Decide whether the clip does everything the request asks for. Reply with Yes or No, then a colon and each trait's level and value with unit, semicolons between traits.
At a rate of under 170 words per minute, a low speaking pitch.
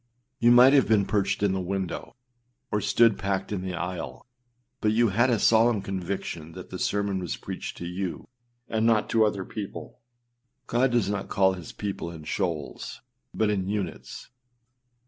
No: average, 175 wpm; low, 100 Hz